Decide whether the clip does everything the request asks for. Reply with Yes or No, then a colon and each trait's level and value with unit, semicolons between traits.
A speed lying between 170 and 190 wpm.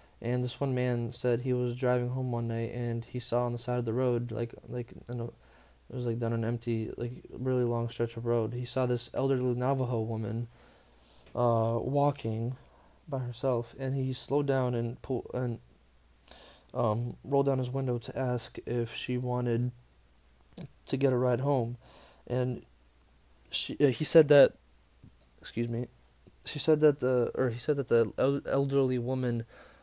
Yes: average, 175 wpm